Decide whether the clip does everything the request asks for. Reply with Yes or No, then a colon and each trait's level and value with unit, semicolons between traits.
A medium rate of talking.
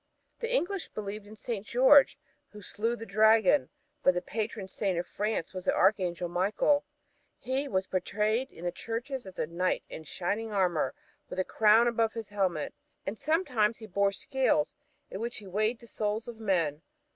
Yes: average, 180 wpm